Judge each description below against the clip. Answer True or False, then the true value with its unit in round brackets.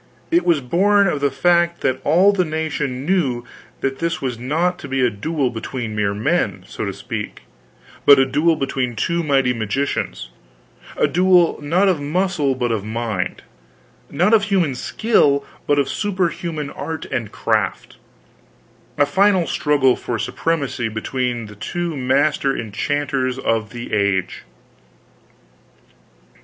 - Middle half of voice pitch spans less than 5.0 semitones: False (5.5 semitones)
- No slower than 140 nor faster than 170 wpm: True (145 wpm)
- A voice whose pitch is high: False (140 Hz)